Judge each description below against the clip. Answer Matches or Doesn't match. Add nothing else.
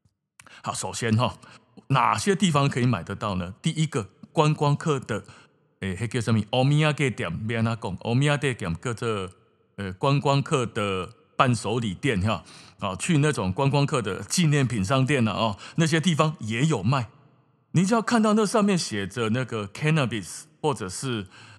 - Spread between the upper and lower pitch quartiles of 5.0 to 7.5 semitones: Matches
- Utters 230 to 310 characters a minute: Matches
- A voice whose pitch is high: Doesn't match